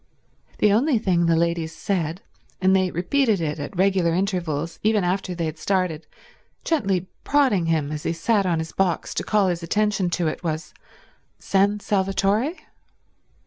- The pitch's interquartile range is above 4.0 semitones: No, average, 3.3 semitones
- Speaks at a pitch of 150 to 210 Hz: Yes, medium, 185 Hz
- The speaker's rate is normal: Yes, average, 160 wpm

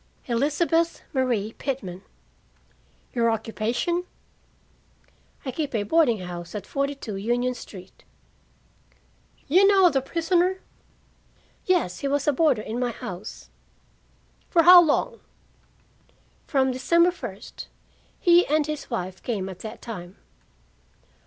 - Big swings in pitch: Yes, wide, 7.4 semitones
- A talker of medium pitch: No, very high, 260 Hz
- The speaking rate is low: Yes, slow, 115 wpm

